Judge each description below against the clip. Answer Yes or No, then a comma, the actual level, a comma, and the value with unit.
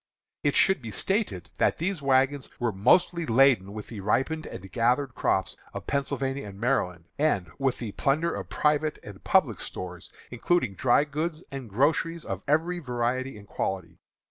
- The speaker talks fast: No, average, 165 wpm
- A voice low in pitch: Yes, low, 130 Hz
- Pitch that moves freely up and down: Yes, wide, 6.5 semitones